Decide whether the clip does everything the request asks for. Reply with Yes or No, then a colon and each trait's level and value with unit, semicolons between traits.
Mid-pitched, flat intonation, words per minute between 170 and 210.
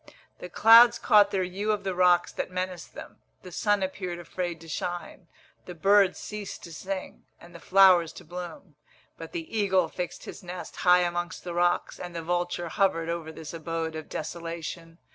Yes: medium, 175 Hz; narrow, 2.1 semitones; average, 180 wpm